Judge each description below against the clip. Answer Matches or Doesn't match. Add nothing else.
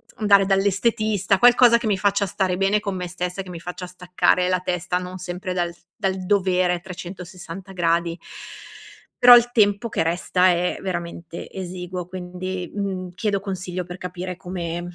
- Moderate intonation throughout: Doesn't match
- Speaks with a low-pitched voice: Doesn't match